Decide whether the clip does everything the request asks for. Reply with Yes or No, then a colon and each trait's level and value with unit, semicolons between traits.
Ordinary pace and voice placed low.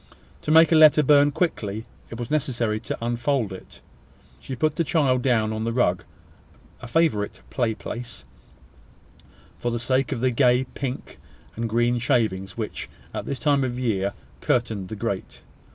Yes: average, 170 wpm; low, 120 Hz